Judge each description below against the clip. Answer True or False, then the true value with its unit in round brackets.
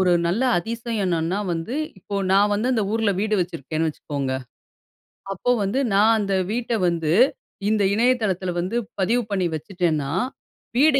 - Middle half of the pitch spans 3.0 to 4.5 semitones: False (4.9 semitones)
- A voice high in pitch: True (195 Hz)